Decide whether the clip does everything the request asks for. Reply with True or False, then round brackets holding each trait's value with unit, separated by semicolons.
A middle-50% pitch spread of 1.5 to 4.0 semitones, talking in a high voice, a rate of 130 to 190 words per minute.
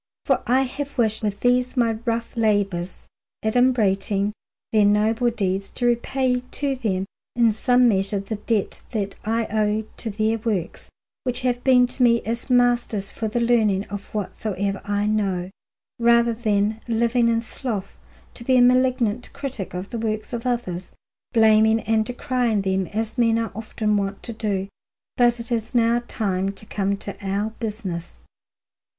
True (2.9 semitones; 220 Hz; 160 wpm)